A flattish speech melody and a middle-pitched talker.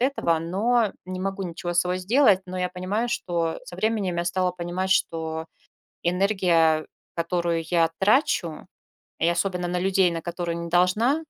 Yes: narrow, 2.2 semitones; medium, 180 Hz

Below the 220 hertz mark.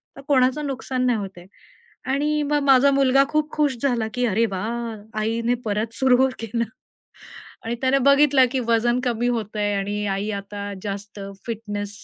No: high, 235 Hz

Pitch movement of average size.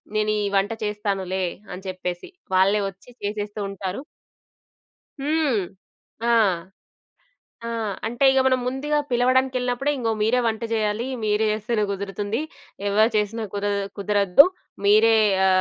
Yes: average, 3.3 semitones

